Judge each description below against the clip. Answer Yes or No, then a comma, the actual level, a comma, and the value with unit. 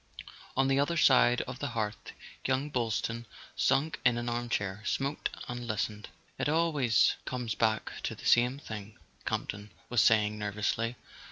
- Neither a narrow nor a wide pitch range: Yes, average, 3.7 semitones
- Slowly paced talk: No, average, 155 wpm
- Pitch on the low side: Yes, low, 120 Hz